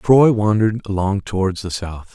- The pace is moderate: Yes, average, 170 wpm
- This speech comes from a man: Yes, male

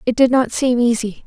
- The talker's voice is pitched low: No, high, 245 Hz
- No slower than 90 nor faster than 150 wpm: No, fast, 240 wpm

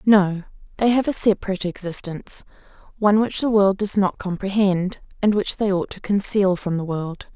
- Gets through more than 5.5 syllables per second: No, 5.3 syllables/s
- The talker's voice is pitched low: No, high, 195 Hz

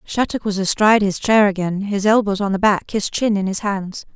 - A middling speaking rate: No, fast, 230 wpm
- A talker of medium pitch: No, high, 200 Hz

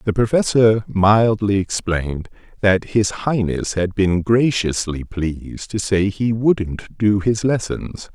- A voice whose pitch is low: Yes, low, 105 Hz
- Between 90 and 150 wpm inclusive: Yes, slow, 135 wpm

